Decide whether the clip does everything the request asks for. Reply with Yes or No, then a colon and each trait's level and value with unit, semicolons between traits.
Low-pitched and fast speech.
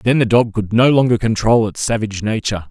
Yes: low, 110 Hz; fast, 220 wpm